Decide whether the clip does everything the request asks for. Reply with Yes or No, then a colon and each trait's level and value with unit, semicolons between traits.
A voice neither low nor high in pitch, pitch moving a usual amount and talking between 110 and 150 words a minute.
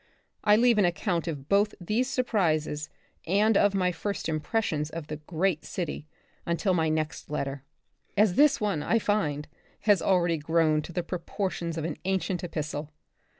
No: medium, 175 Hz; average, 4.6 semitones; average, 165 wpm